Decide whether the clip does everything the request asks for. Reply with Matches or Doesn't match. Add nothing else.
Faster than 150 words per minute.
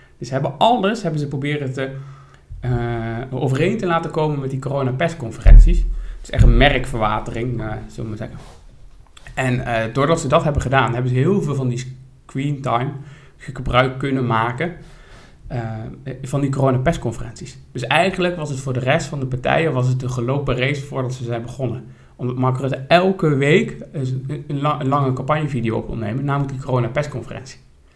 Matches